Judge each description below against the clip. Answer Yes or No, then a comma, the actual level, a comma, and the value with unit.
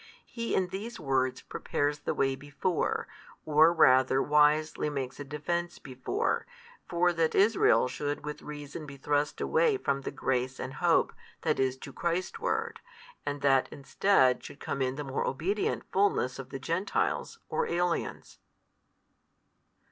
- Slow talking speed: No, average, 150 wpm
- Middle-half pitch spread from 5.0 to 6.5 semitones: No, average, 4.3 semitones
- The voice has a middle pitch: Yes, medium, 145 Hz